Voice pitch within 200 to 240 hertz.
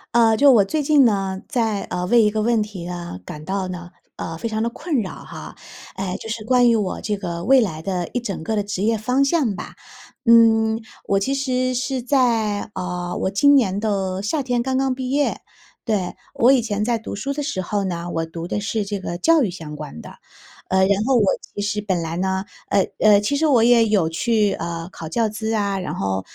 Yes: high, 210 Hz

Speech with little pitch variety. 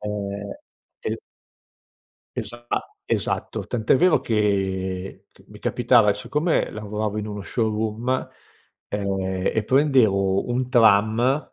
No: average, 3.3 semitones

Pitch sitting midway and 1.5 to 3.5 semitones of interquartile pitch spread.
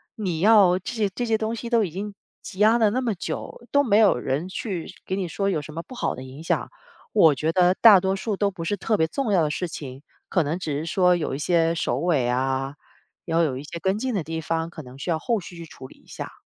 No: medium, 180 Hz; average, 4.7 semitones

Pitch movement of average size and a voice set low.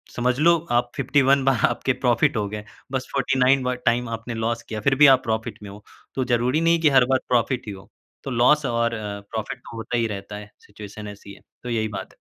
Yes: average, 3.3 semitones; low, 120 Hz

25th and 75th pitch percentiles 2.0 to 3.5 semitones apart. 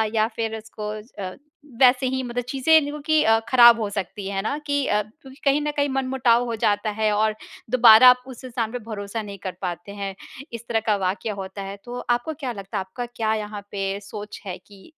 No: average, 3.9 semitones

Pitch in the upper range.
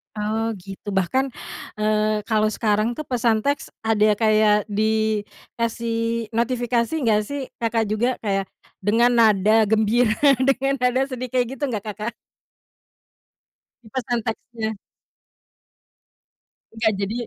Yes: high, 225 Hz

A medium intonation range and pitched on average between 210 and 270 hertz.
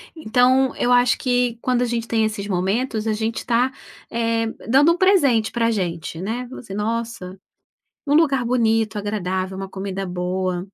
Yes: average, 4.1 semitones; high, 225 Hz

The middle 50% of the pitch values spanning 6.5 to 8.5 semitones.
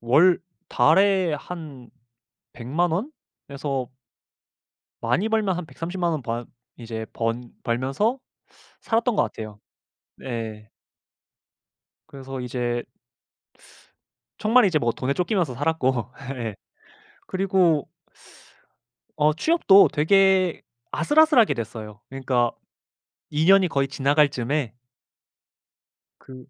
Yes: wide, 7.3 semitones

